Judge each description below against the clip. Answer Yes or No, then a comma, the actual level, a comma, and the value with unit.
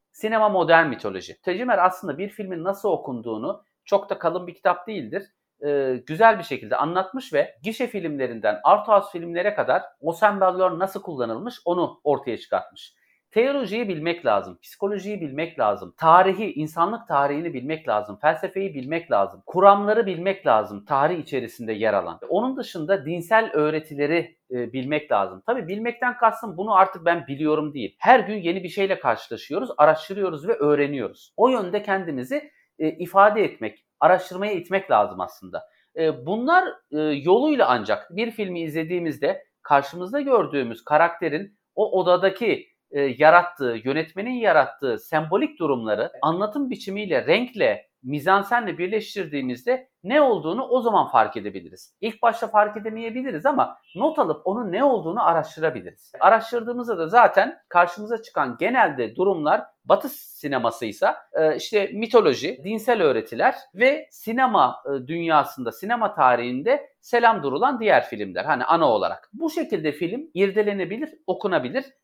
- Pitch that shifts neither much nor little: No, wide, 6.2 semitones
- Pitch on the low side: No, high, 190 Hz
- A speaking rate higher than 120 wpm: Yes, average, 130 wpm